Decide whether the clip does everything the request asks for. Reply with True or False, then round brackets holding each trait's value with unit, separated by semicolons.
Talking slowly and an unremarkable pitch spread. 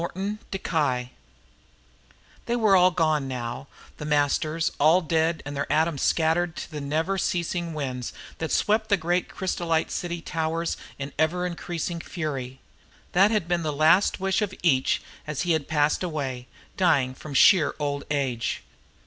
False (150 wpm; 3.5 semitones)